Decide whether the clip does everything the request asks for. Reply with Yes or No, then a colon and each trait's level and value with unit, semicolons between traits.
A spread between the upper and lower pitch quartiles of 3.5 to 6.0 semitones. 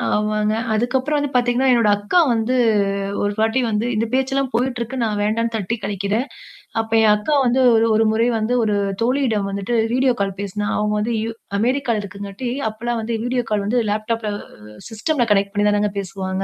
No: average, 2.9 semitones